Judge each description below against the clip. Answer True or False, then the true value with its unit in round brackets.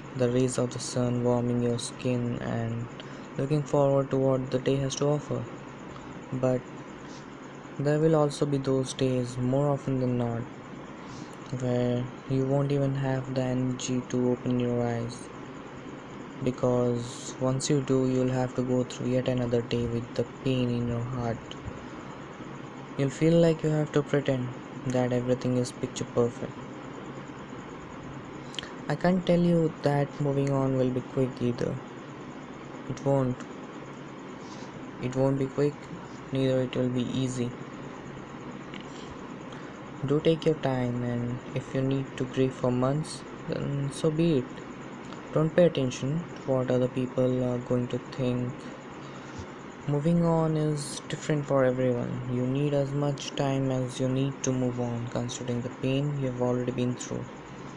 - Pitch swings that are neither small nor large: False (2.1 semitones)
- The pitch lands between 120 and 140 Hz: True (130 Hz)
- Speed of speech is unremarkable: True (150 wpm)